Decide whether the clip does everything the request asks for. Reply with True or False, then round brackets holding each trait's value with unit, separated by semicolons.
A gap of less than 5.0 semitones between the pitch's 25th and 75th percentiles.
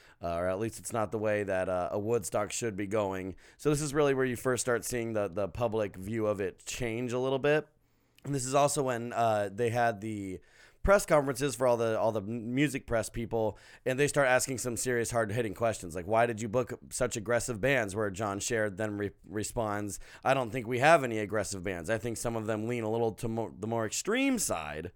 True (3.1 semitones)